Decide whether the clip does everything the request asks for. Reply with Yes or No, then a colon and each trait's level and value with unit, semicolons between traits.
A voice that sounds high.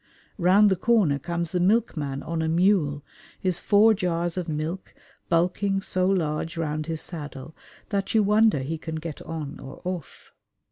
No: medium, 170 Hz